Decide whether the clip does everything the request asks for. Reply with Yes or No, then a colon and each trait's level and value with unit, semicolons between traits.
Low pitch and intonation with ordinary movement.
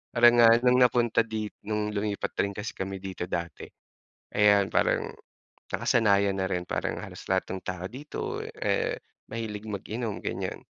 Yes: low, 105 Hz; average, 3.2 semitones